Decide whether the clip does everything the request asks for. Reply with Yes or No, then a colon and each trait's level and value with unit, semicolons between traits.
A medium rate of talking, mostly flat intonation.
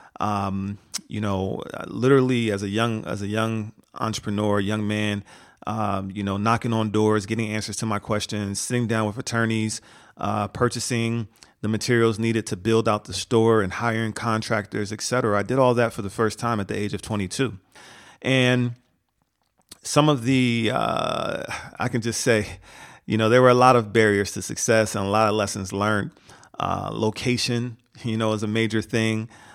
Yes: average, 180 wpm; narrow, 2.2 semitones